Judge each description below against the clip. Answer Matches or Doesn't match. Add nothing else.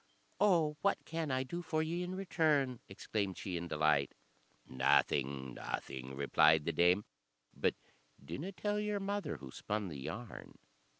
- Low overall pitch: Matches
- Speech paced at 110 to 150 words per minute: Matches